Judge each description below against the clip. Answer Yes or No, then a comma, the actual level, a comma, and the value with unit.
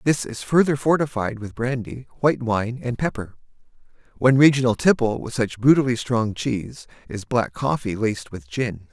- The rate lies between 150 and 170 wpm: Yes, average, 160 wpm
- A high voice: No, low, 120 Hz